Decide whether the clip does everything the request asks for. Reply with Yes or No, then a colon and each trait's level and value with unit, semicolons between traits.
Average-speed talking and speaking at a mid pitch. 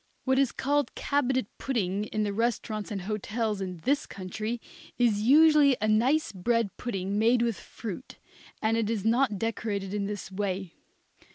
No: average, 160 wpm; high, 220 Hz